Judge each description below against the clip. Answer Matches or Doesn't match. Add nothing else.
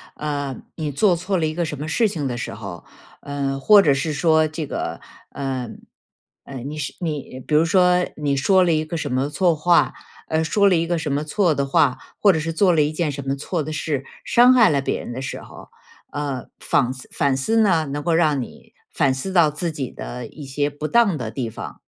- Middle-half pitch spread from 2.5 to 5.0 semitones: Matches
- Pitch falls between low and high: Matches